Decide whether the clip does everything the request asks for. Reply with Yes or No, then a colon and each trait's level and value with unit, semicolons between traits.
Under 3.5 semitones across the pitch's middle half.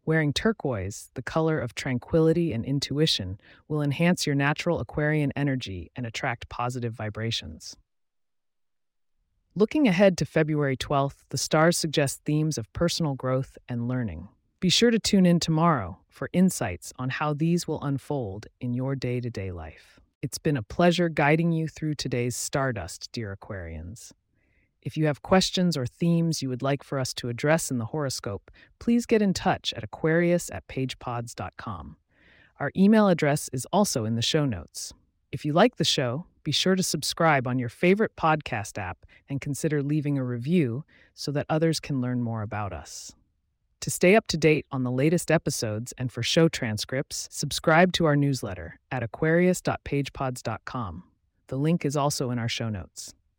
No: average, 5.3 semitones